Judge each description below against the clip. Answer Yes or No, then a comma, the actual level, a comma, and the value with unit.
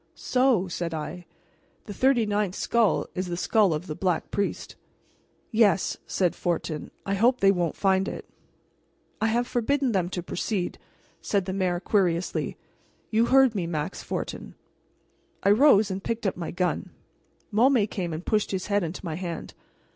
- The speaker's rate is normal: Yes, average, 160 wpm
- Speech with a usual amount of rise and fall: Yes, average, 3.8 semitones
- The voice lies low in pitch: No, high, 195 Hz